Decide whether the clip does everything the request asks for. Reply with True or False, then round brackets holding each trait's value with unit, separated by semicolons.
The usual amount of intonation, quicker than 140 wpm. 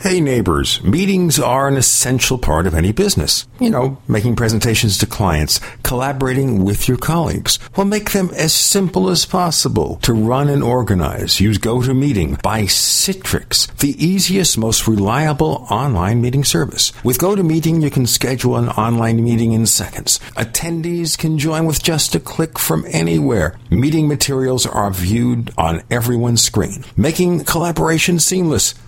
False (6.2 semitones; 150 wpm)